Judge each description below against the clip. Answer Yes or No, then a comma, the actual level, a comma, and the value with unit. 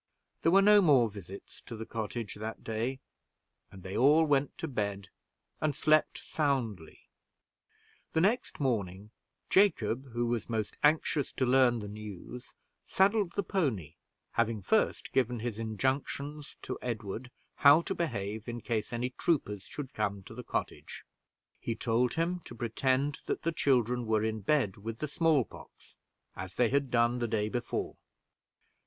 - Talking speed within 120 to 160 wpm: Yes, average, 155 wpm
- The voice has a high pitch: No, low, 120 Hz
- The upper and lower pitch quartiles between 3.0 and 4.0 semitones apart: No, average, 4.8 semitones